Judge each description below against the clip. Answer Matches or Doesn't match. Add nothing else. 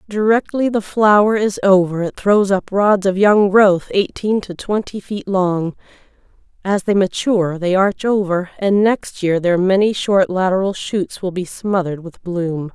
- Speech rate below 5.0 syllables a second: Matches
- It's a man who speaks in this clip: Doesn't match